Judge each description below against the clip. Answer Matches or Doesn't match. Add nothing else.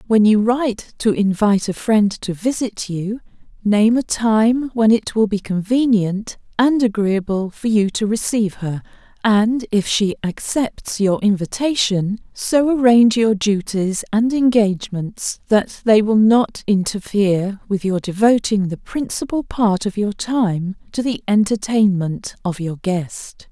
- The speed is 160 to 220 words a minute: Doesn't match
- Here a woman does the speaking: Matches